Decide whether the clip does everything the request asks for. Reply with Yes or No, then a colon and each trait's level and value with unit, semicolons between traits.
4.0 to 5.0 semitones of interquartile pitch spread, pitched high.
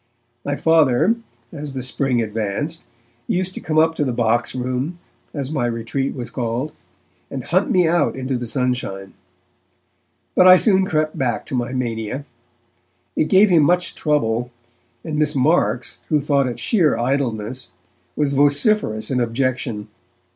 No: average, 4.5 semitones; low, 135 Hz